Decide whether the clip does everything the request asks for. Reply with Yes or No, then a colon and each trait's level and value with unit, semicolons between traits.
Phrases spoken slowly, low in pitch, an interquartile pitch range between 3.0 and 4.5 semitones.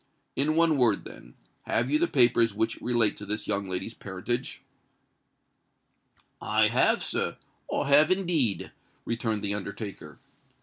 No: slow, 125 wpm; low, 115 Hz; wide, 5.4 semitones